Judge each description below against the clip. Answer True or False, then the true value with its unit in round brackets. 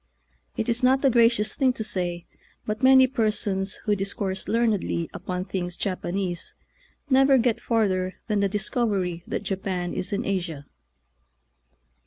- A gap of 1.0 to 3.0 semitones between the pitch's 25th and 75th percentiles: False (4.0 semitones)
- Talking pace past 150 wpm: False (140 wpm)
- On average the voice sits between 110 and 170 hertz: False (200 Hz)